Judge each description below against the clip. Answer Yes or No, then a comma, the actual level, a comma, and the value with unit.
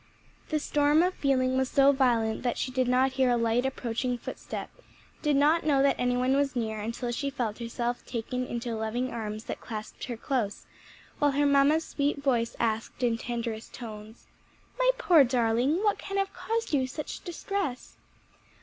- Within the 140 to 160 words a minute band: No, average, 175 wpm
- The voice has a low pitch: No, very high, 255 Hz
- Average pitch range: Yes, average, 3.4 semitones